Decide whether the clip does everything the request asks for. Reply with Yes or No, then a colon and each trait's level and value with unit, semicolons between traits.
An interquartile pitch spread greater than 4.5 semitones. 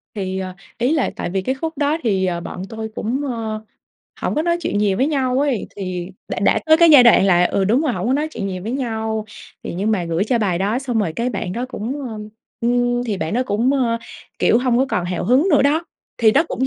Yes: average, 5.1 semitones